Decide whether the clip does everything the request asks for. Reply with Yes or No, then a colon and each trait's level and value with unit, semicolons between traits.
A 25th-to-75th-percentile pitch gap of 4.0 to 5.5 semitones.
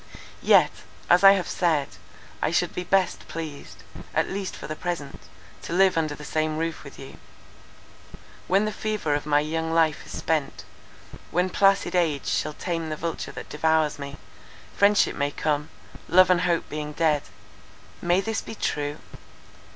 No: average, 3.3 semitones